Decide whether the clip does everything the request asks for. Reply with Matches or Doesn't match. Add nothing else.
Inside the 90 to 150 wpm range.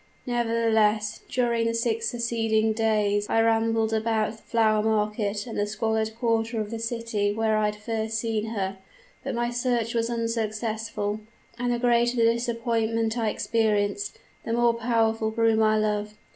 Doesn't match